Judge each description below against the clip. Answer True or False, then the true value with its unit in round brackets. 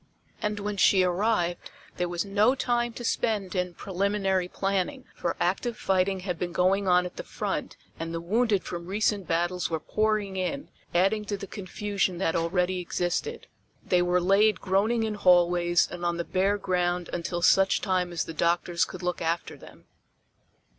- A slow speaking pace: False (175 wpm)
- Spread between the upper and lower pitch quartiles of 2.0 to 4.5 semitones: True (2.6 semitones)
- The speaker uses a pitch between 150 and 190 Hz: True (185 Hz)